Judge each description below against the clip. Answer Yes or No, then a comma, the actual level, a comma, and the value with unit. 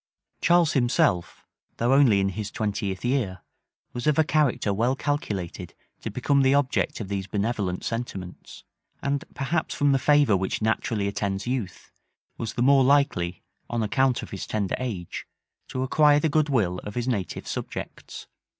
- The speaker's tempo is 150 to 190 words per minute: Yes, average, 160 wpm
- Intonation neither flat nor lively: No, wide, 5.8 semitones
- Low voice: Yes, low, 120 Hz